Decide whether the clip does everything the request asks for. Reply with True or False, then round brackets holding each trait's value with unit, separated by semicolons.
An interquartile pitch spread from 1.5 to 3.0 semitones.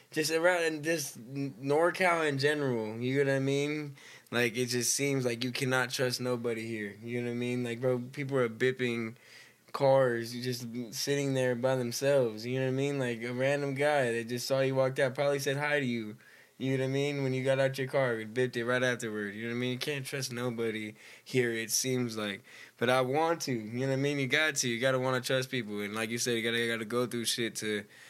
True (2.6 semitones)